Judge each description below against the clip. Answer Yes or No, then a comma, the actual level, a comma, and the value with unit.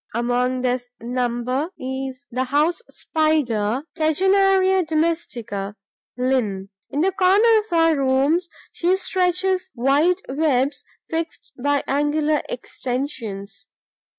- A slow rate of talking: Yes, slow, 100 wpm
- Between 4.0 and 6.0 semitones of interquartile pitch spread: Yes, average, 5.3 semitones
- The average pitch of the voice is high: Yes, very high, 285 Hz